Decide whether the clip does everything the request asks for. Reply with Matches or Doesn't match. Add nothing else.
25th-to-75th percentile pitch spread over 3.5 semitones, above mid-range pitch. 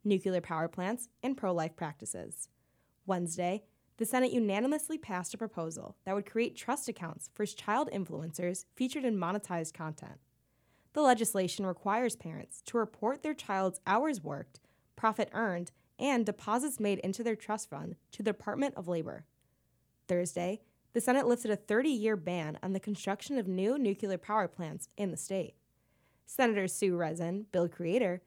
Matches